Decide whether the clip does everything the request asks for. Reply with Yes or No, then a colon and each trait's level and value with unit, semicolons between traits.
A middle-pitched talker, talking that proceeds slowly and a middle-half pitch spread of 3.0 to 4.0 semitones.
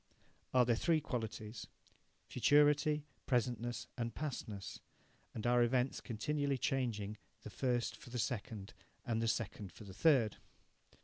No: low, 120 Hz; slow, 130 wpm; average, 3.4 semitones